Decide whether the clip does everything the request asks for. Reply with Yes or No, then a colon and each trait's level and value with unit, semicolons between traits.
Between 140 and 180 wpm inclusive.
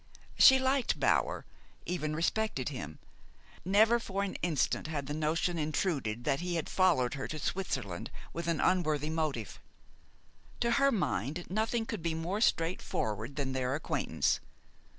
Yes: average, 145 wpm